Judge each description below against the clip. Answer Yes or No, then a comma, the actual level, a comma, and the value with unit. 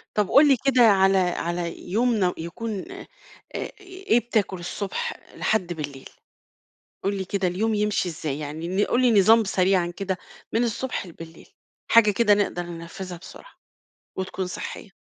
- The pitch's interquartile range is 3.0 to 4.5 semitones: Yes, average, 4.2 semitones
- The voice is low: No, high, 195 Hz